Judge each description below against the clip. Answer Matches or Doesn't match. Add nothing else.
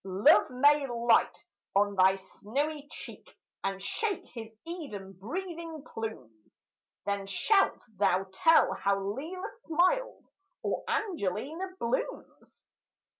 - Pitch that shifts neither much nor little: Doesn't match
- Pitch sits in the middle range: Doesn't match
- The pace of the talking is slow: Matches